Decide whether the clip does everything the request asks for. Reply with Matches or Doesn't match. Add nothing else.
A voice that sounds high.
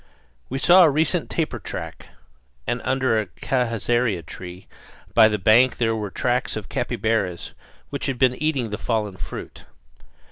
Doesn't match